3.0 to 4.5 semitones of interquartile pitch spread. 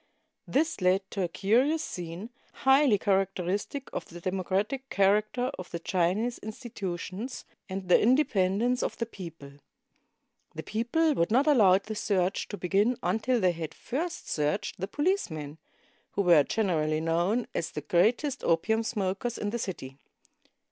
No: wide, 5.4 semitones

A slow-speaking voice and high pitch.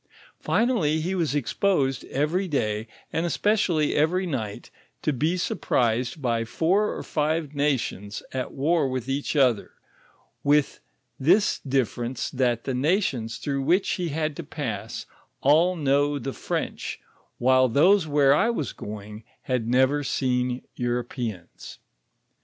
No: slow, 130 wpm; medium, 140 Hz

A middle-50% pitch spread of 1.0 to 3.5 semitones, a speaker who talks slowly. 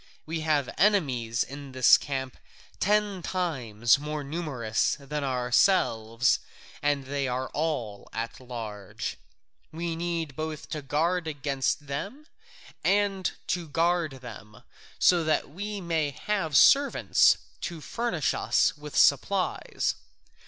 No: average, 5.0 semitones; slow, 115 wpm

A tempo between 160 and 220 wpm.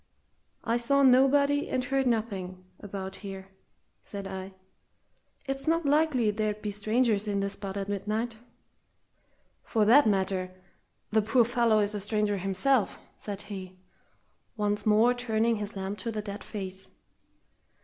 No: average, 140 wpm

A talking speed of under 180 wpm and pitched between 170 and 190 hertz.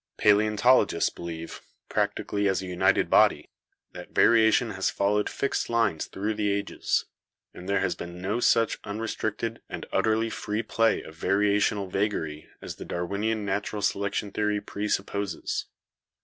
No: average, 145 wpm; low, 105 Hz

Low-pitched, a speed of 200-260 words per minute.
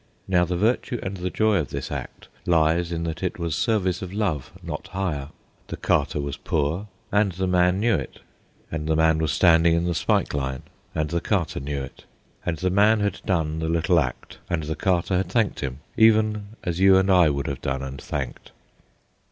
Yes: very low, 85 Hz; fast, 205 wpm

